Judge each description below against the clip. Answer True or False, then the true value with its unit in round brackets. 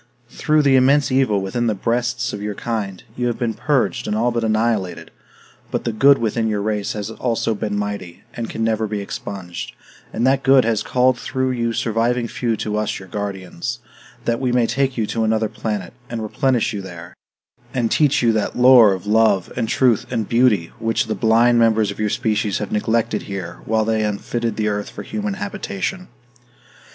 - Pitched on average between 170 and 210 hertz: False (110 Hz)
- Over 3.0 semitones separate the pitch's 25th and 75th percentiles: False (2.7 semitones)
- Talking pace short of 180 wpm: False (195 wpm)